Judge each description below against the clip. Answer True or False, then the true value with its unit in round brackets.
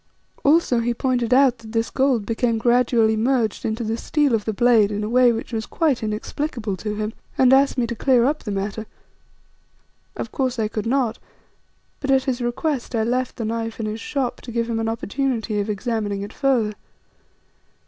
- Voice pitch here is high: True (235 Hz)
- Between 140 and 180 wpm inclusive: False (195 wpm)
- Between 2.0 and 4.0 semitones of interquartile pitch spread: True (2.7 semitones)